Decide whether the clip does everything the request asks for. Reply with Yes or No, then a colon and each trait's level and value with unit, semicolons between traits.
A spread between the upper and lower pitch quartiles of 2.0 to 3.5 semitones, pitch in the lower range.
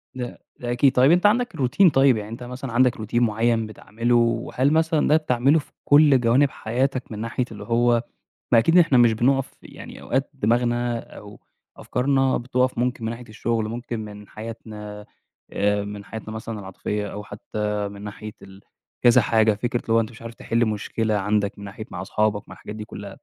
Yes: average, 2.9 semitones; low, 115 Hz